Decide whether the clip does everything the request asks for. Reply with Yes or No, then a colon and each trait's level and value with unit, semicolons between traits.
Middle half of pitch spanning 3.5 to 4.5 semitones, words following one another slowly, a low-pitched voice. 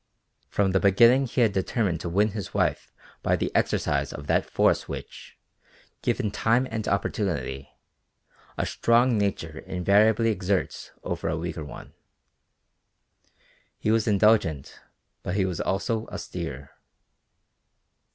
Yes: average, 4.0 semitones; slow, 125 wpm; low, 100 Hz